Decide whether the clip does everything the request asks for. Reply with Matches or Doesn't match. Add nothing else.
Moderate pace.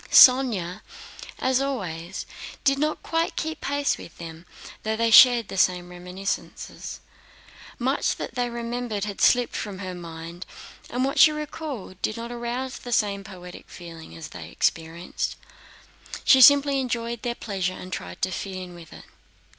Matches